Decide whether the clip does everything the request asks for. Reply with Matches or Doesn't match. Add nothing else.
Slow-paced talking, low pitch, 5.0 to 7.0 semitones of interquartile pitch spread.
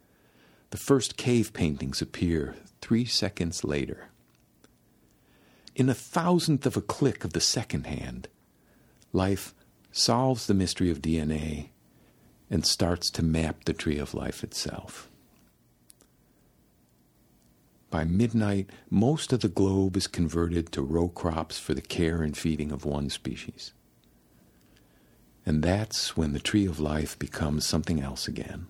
Matches